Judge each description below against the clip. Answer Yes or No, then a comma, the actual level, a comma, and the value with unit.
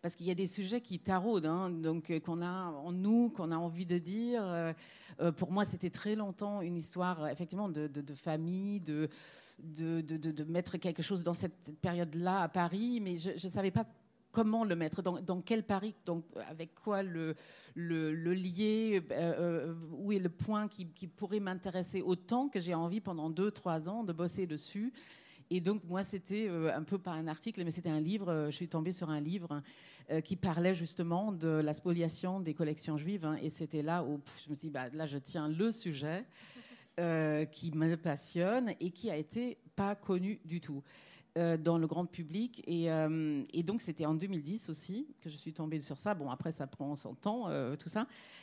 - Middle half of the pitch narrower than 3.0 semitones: No, average, 3.6 semitones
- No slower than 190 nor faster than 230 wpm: Yes, average, 205 wpm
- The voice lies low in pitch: No, medium, 175 Hz